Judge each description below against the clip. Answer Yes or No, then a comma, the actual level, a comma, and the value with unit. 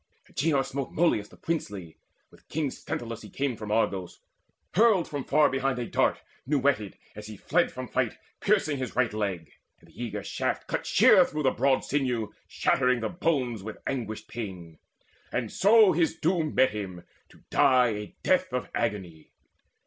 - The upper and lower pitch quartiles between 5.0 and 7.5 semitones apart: Yes, wide, 5.5 semitones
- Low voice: Yes, low, 125 Hz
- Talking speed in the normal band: Yes, average, 170 wpm